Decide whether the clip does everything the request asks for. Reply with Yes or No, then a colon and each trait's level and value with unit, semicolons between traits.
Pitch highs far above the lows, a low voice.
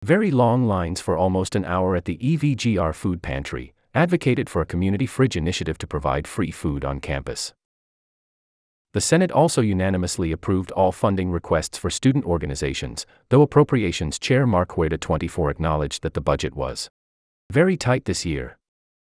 Yes: wide, 7.7 semitones; very low, 90 Hz